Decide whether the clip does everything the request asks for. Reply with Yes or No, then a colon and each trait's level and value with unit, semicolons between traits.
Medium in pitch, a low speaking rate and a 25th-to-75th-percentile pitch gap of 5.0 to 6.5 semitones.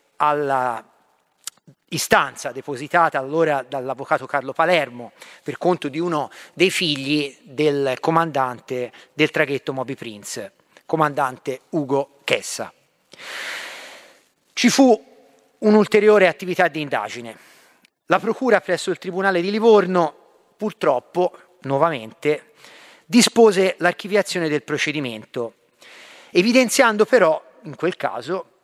Yes: medium, 155 Hz; slow, 95 wpm; wide, 5.5 semitones